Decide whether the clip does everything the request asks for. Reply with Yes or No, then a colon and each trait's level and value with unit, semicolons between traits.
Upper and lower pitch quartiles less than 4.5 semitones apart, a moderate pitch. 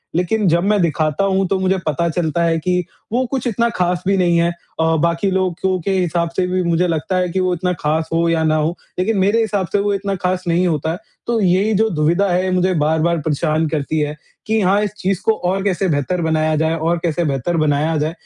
Yes: average, 3.0 semitones; medium, 175 Hz